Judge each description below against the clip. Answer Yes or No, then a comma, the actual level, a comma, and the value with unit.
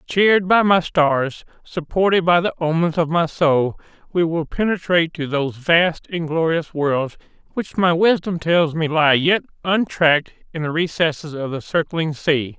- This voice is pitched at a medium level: Yes, medium, 165 Hz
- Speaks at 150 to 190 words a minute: Yes, average, 165 wpm